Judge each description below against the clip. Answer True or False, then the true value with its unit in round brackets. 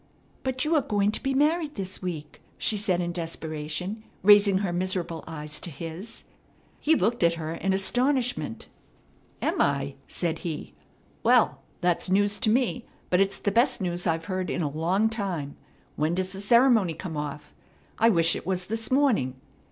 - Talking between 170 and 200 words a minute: True (175 wpm)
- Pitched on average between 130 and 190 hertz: True (185 Hz)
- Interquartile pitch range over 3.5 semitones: True (5.2 semitones)